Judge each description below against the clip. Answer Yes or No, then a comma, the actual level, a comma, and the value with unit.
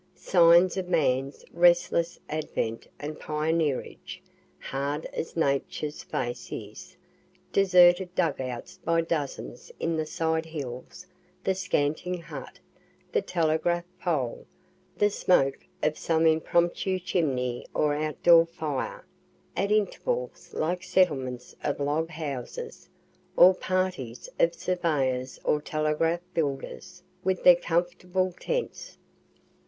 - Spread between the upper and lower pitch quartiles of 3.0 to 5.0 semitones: Yes, average, 3.4 semitones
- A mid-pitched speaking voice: Yes, medium, 165 Hz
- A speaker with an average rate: No, slow, 110 wpm